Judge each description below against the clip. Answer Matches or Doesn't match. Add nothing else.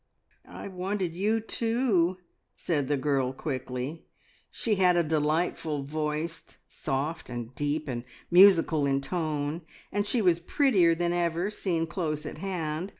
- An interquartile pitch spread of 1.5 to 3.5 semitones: Doesn't match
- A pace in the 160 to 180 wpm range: Doesn't match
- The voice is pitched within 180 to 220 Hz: Doesn't match